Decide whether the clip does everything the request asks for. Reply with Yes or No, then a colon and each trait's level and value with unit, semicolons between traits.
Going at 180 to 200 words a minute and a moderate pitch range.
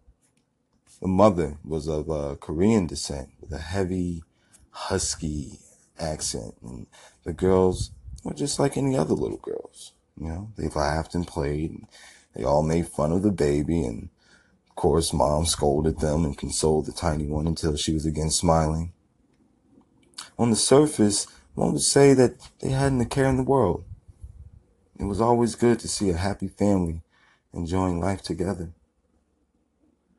No: average, 155 wpm; average, 4.1 semitones